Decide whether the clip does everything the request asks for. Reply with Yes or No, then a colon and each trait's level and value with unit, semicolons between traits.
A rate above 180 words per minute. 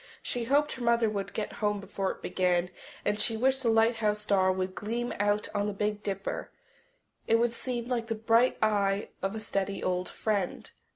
Yes: average, 190 wpm